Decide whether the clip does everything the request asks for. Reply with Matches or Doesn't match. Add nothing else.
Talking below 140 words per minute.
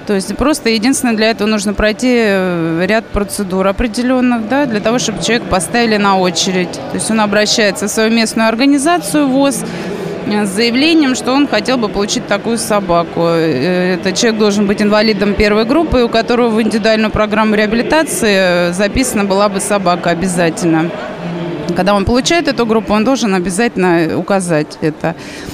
Doesn't match